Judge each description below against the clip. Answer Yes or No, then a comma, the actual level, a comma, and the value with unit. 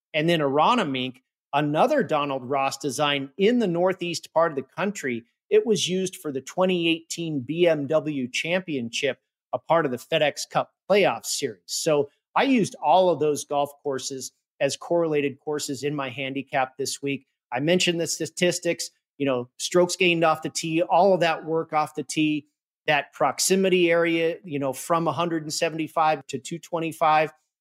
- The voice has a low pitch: No, medium, 155 Hz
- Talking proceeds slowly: No, average, 160 wpm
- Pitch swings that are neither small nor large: Yes, average, 3.3 semitones